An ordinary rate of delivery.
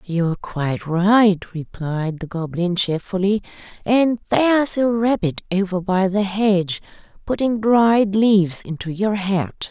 No: slow, 130 wpm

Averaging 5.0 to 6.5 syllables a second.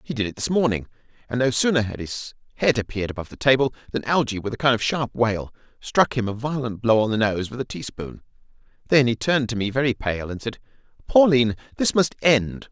Yes: 6.1 syllables/s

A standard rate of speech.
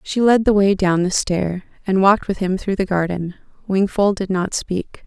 No: fast, 215 wpm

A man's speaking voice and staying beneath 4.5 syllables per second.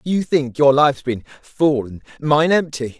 Yes: male; 4.3 syllables/s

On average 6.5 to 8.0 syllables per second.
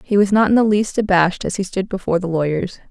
Yes: 6.6 syllables/s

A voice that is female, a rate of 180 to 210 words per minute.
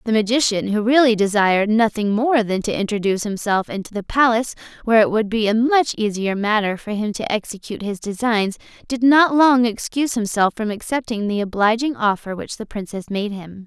Yes: female; average, 190 wpm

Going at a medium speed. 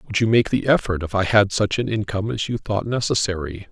No: fast, 240 wpm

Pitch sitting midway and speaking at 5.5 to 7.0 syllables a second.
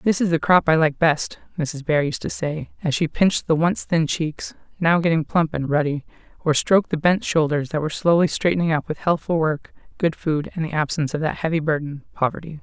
Yes: medium, 160 Hz; 5.6 syllables/s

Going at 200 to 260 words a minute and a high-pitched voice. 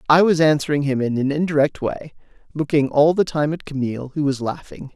No: fast, 205 wpm; medium, 145 Hz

